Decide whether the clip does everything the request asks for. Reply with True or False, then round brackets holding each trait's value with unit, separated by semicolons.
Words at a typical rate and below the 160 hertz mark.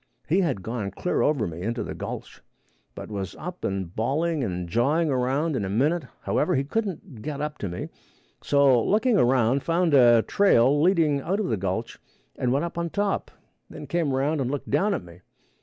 True (195 wpm; 140 Hz)